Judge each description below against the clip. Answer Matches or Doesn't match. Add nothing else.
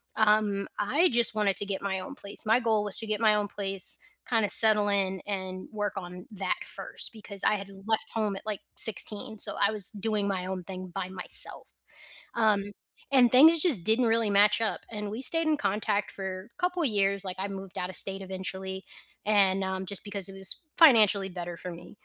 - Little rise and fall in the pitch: Matches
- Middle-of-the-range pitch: Doesn't match